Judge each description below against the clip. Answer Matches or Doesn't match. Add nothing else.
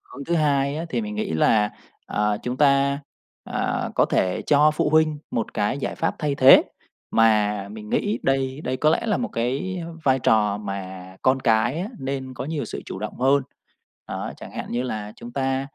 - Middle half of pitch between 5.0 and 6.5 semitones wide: Matches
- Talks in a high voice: Doesn't match